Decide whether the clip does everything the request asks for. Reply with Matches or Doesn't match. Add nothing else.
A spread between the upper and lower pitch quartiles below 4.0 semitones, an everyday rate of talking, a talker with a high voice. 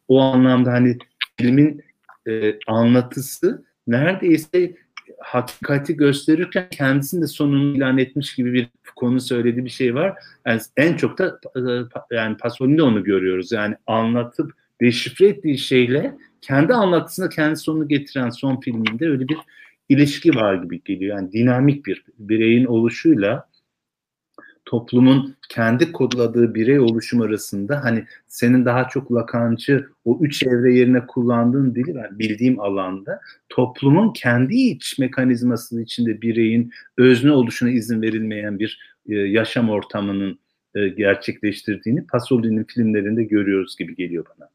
Doesn't match